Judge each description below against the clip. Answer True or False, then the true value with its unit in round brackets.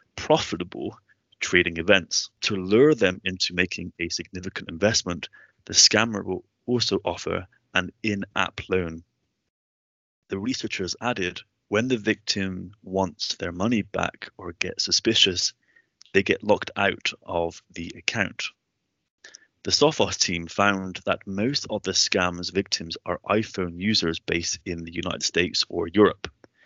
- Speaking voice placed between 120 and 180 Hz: False (95 Hz)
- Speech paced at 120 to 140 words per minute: True (135 wpm)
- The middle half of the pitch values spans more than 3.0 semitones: False (2.7 semitones)